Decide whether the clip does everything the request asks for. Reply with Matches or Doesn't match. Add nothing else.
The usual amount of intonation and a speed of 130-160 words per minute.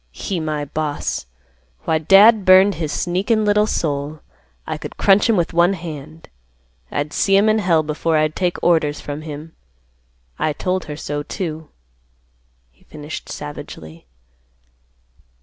Matches